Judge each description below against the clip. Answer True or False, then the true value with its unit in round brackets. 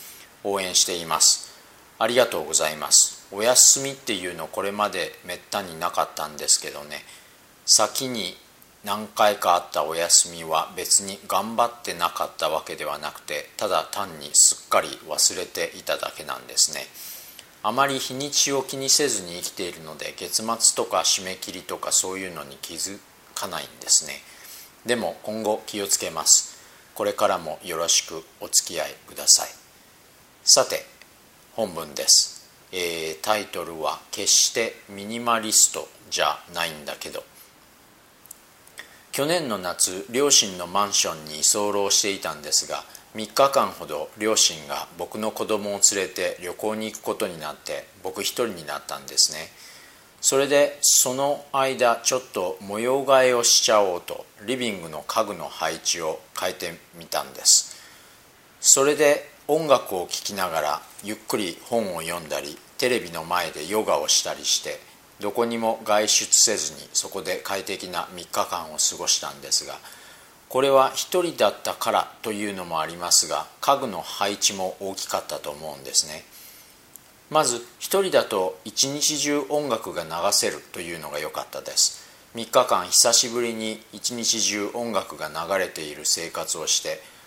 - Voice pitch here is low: True (110 Hz)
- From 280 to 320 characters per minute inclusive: True (295 characters per minute)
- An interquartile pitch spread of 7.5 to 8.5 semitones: False (5.1 semitones)